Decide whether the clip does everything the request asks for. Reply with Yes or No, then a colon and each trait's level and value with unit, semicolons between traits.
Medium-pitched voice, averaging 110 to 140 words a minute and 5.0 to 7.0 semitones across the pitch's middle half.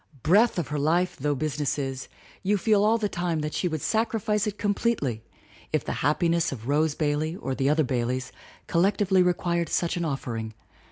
No: medium, 160 Hz; average, 185 wpm; wide, 5.4 semitones